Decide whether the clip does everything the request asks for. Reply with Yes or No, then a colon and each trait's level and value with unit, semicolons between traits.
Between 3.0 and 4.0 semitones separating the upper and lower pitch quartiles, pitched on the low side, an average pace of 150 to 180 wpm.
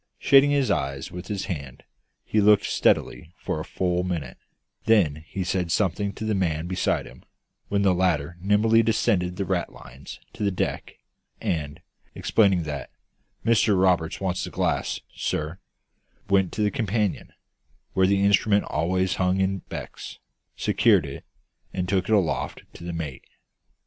Yes: average, 3.4 semitones; very low, 95 Hz; average, 155 wpm